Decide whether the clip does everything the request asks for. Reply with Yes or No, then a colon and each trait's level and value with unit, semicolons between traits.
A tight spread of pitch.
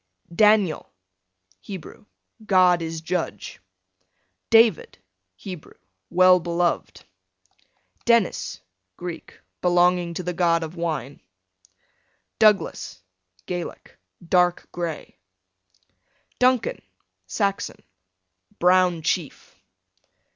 Yes: narrow, 2.0 semitones